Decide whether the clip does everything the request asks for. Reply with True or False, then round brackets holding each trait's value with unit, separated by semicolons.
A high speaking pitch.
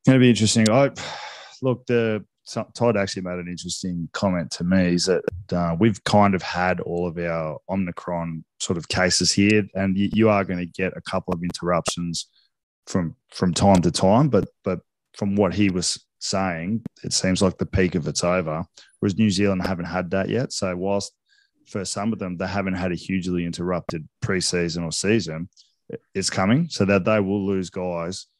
False (95 Hz)